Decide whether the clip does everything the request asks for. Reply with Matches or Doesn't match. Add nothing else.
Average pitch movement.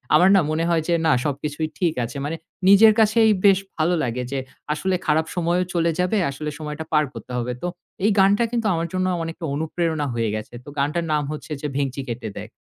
Matches